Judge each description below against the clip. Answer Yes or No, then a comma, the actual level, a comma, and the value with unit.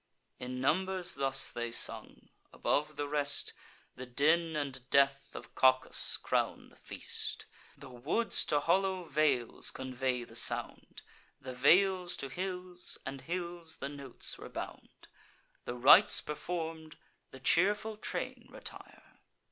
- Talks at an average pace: No, slow, 125 wpm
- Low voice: No, medium, 145 Hz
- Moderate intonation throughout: Yes, average, 5.0 semitones